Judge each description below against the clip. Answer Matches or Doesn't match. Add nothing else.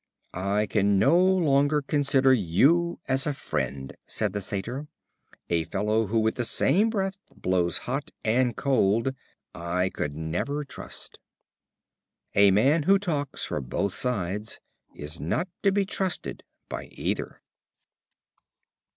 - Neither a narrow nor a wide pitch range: Doesn't match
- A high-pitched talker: Doesn't match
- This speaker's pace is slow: Matches